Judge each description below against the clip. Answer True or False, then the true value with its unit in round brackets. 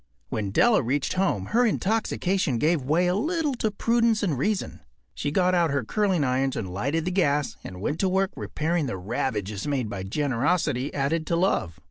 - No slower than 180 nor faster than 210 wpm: True (185 wpm)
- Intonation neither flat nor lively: False (7.1 semitones)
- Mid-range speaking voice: True (155 Hz)